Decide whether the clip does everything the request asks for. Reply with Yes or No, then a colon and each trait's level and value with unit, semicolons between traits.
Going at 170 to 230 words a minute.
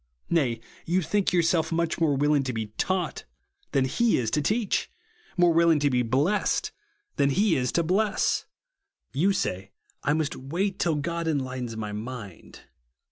No: average, 160 wpm